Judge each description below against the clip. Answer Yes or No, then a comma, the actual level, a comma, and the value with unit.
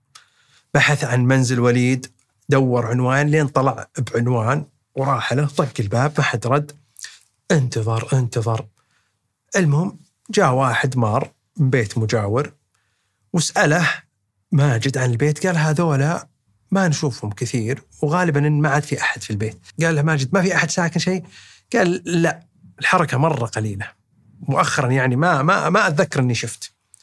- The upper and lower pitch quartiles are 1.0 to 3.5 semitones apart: No, average, 4.5 semitones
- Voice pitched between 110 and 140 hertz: Yes, low, 135 Hz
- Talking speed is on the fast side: Yes, fast, 140 wpm